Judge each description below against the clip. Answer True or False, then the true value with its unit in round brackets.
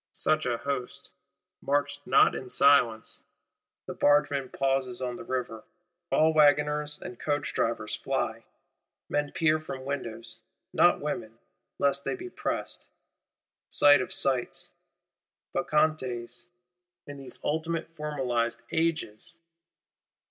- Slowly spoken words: True (105 wpm)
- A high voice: False (140 Hz)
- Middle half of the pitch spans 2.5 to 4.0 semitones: True (3.2 semitones)